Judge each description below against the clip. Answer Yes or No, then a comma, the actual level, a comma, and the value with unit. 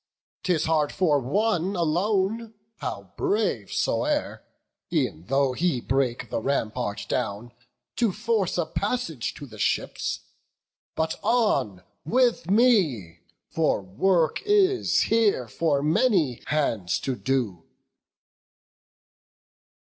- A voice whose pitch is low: No, medium, 155 Hz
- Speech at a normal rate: No, slow, 105 wpm